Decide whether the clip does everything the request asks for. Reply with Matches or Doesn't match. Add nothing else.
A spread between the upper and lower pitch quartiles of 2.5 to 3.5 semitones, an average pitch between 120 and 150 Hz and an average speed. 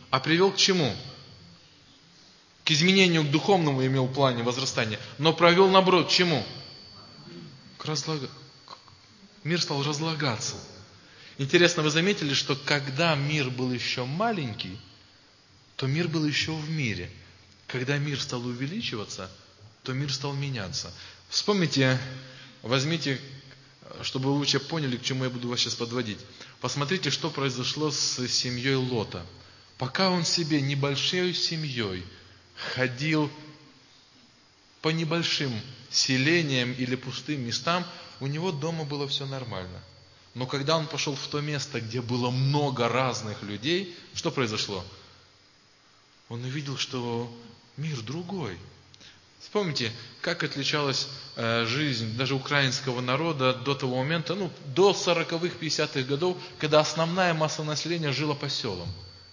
Doesn't match